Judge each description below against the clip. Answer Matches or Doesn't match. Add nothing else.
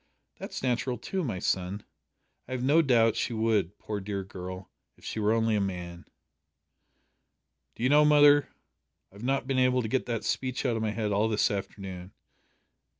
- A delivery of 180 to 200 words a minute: Matches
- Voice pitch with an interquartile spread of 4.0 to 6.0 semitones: Matches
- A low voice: Matches